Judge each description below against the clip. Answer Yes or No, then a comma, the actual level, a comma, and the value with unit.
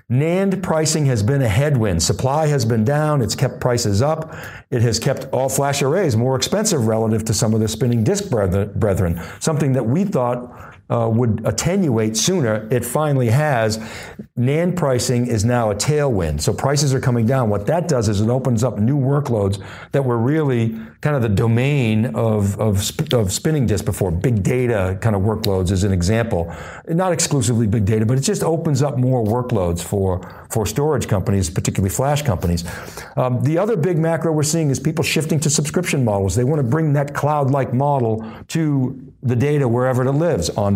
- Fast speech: No, average, 190 wpm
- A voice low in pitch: Yes, low, 125 Hz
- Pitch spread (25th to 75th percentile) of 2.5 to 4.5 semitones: No, average, 4.9 semitones